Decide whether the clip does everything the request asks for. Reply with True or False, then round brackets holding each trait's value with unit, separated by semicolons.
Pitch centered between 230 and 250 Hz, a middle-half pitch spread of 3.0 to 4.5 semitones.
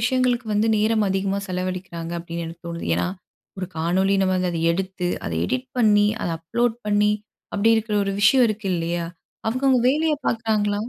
False (200 Hz; 4.2 semitones)